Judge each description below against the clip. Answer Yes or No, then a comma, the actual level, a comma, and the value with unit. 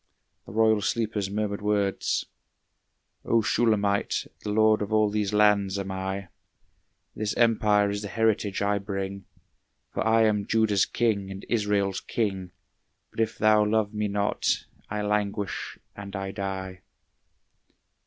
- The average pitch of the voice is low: Yes, low, 105 Hz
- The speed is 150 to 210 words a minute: No, slow, 135 wpm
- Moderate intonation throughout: No, narrow, 1.5 semitones